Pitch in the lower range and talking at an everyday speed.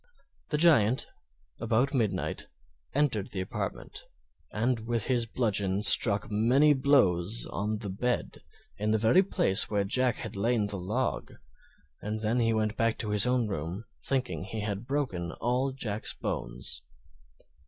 Yes: low, 110 Hz; average, 145 wpm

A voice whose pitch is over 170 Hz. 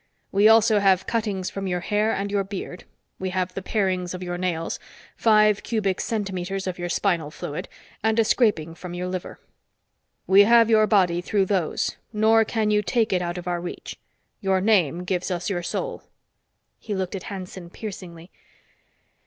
Yes: high, 190 Hz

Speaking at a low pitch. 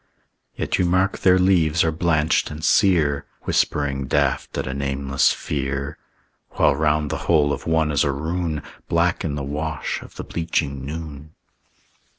Yes: very low, 75 Hz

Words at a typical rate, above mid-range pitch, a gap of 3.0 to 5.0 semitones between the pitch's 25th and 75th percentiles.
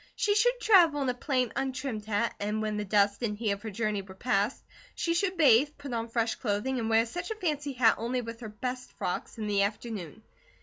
No: fast, 225 wpm; high, 230 Hz; average, 4.6 semitones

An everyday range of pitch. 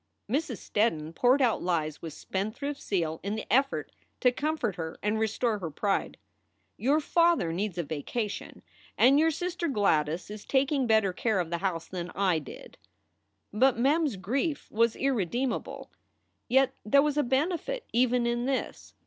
No: wide, 6.7 semitones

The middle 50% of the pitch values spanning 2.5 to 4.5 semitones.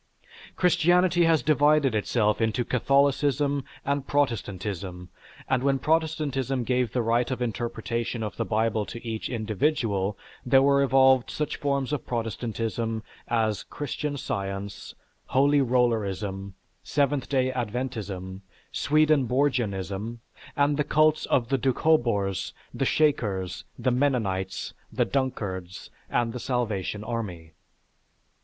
No: average, 4.9 semitones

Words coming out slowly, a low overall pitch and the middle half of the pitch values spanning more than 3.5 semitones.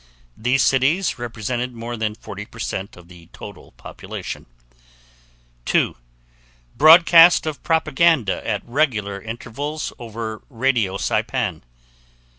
Yes: slow, 95 wpm; low, 120 Hz; average, 5.2 semitones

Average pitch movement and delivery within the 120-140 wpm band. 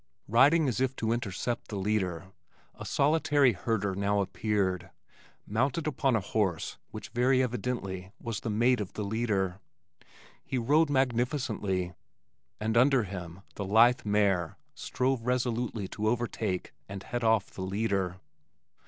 Yes: average, 4.3 semitones; slow, 135 wpm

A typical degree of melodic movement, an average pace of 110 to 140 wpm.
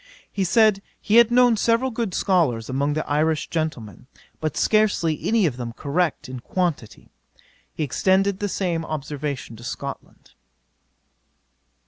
No: wide, 6.2 semitones; slow, 135 wpm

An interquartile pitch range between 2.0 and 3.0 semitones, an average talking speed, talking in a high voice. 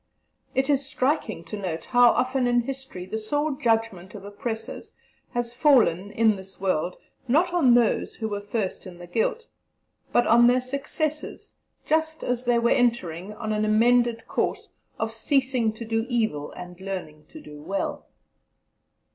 No: average, 4.4 semitones; average, 160 wpm; high, 230 Hz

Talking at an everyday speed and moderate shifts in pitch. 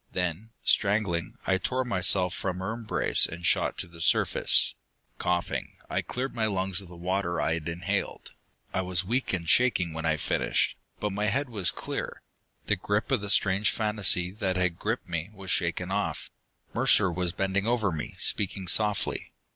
Yes: average, 175 wpm; average, 3.1 semitones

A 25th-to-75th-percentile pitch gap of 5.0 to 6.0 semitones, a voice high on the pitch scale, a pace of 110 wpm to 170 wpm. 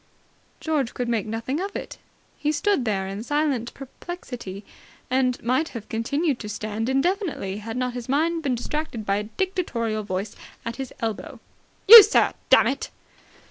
Yes: wide, 5.6 semitones; very high, 250 Hz; average, 155 wpm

